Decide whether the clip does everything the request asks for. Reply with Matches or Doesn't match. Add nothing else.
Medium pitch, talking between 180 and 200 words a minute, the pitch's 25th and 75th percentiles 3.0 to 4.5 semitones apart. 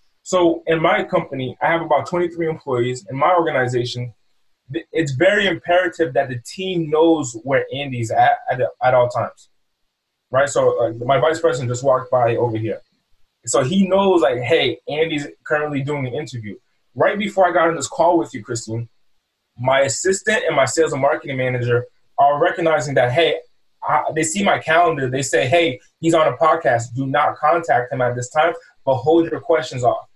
Doesn't match